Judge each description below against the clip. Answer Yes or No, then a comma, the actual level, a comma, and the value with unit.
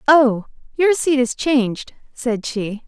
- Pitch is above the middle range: Yes, very high, 255 Hz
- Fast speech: No, average, 145 wpm